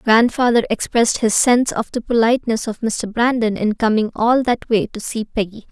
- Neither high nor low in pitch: No, high, 225 Hz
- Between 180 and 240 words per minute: Yes, average, 190 wpm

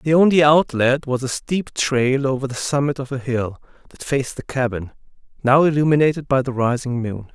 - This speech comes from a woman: No, male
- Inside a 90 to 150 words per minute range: No, average, 190 wpm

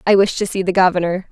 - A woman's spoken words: Yes, female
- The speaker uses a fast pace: Yes, fast, 275 wpm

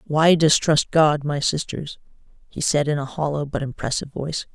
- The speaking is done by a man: No, female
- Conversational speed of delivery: Yes, average, 170 wpm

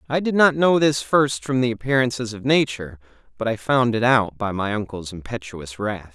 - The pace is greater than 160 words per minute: Yes, fast, 205 wpm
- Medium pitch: No, low, 120 Hz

